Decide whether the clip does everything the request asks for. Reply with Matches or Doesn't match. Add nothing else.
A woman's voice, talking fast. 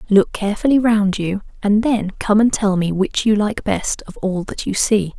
Matches